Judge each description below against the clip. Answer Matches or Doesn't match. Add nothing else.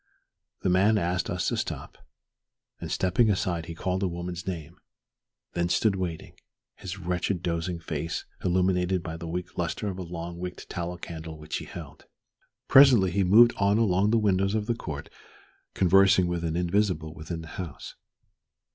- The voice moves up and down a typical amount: Doesn't match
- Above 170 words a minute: Doesn't match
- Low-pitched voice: Matches